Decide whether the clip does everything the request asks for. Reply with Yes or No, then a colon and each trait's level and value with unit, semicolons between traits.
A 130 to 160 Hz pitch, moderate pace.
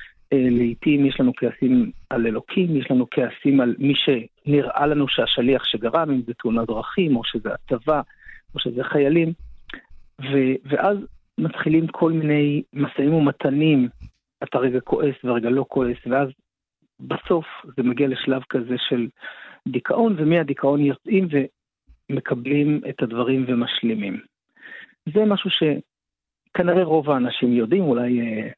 Yes: low, 135 Hz; average, 125 wpm